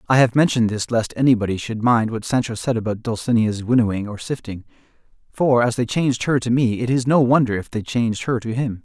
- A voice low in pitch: Yes, low, 115 Hz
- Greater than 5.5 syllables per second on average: Yes, 6.0 syllables/s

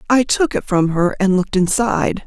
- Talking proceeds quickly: Yes, fast, 210 wpm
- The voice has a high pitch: Yes, high, 205 Hz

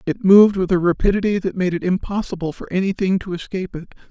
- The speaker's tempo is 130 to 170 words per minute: No, fast, 205 wpm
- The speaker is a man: Yes, male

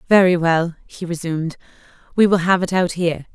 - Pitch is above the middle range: No, medium, 175 Hz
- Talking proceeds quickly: No, average, 180 wpm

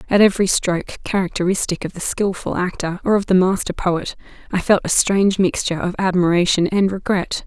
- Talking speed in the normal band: Yes, average, 175 wpm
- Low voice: No, medium, 185 Hz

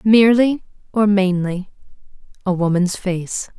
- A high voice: Yes, high, 195 Hz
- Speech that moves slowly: Yes, slow, 100 wpm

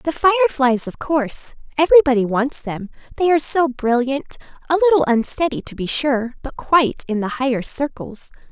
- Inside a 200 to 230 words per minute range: No, average, 155 wpm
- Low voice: No, very high, 275 Hz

